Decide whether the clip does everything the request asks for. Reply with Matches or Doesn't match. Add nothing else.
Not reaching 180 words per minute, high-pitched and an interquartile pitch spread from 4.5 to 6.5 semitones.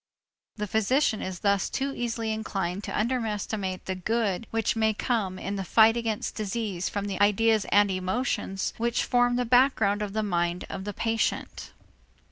Doesn't match